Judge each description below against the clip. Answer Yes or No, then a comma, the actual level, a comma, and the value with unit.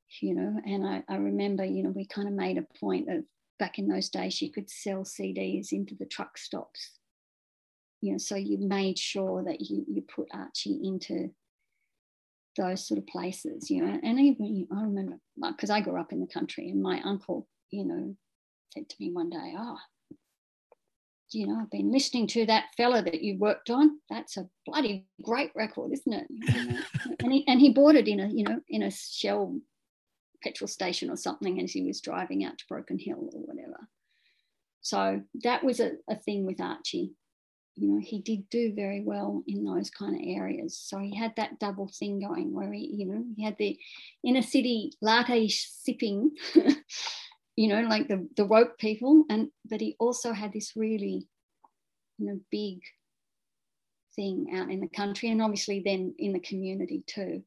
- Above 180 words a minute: Yes, average, 190 wpm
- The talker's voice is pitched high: Yes, high, 215 Hz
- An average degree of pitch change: No, wide, 5.9 semitones